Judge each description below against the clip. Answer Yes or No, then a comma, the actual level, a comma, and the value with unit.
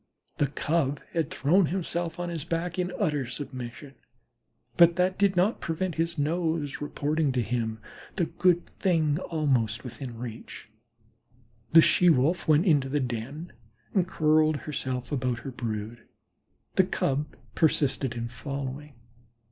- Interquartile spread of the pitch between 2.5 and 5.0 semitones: Yes, average, 4.7 semitones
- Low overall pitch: No, medium, 150 Hz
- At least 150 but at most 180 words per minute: No, average, 140 wpm